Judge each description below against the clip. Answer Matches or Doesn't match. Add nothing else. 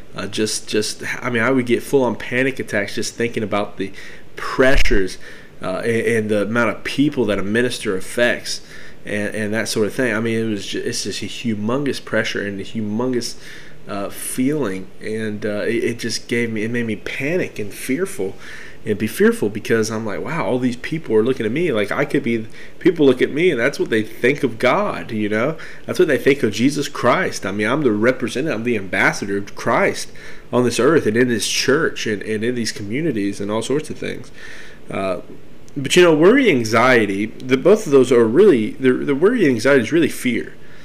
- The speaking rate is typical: Doesn't match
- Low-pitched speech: Matches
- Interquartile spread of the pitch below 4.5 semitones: Matches